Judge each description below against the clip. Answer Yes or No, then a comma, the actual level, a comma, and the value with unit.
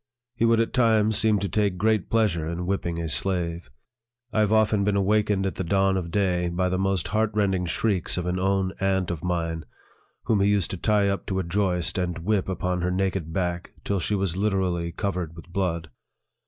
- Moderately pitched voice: No, very low, 95 Hz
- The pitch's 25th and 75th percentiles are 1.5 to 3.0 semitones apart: Yes, average, 2.7 semitones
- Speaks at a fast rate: Yes, fast, 210 wpm